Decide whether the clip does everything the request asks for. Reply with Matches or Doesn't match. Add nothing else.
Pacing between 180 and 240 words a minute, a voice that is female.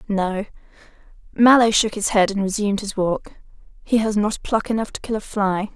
Matches